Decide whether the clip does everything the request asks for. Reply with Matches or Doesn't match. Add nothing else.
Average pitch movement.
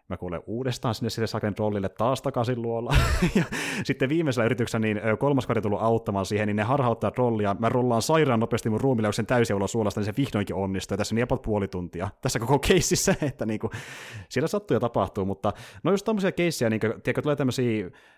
Matches